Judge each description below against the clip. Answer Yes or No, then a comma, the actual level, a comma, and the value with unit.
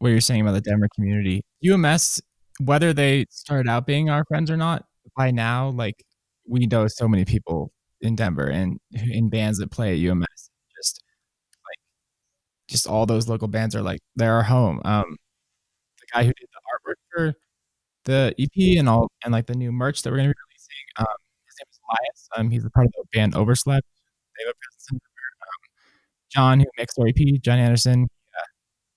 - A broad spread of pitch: No, average, 3.9 semitones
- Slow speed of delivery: No, average, 190 wpm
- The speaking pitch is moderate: No, low, 120 Hz